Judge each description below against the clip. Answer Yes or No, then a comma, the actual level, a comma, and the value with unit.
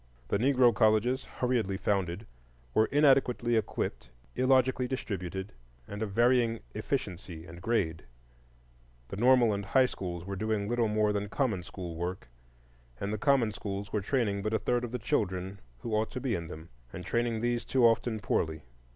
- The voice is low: Yes, low, 110 Hz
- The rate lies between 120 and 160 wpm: No, average, 170 wpm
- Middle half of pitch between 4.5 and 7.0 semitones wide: No, average, 4.0 semitones